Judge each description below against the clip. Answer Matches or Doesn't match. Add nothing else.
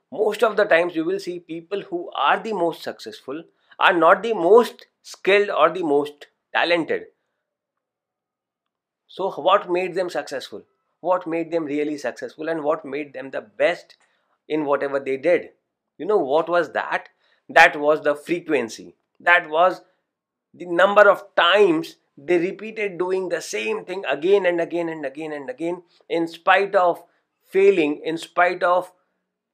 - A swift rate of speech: Doesn't match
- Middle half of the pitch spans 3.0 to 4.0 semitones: Doesn't match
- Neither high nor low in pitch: Matches